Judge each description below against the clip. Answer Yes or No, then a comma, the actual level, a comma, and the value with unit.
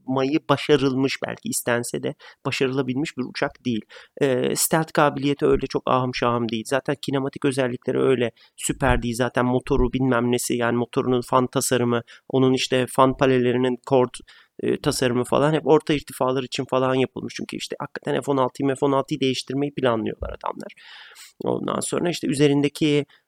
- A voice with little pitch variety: Yes, narrow, 2.1 semitones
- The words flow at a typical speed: No, fast, 145 wpm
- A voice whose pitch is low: Yes, low, 130 Hz